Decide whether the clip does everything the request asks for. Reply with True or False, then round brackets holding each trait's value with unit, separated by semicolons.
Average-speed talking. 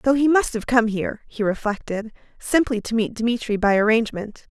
True (185 wpm)